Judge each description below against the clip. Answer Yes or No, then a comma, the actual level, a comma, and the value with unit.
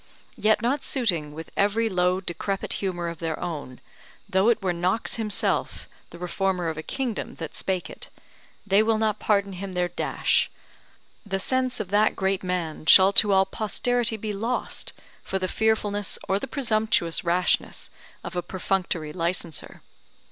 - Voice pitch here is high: Yes, high, 195 Hz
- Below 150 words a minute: No, average, 160 wpm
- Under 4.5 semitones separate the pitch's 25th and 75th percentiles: Yes, average, 3.5 semitones